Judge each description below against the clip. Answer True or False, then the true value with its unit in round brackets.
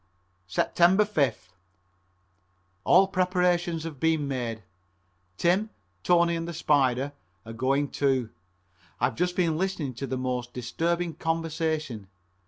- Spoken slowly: True (120 wpm)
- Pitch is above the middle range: False (155 Hz)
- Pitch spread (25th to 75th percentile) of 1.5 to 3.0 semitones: False (5.1 semitones)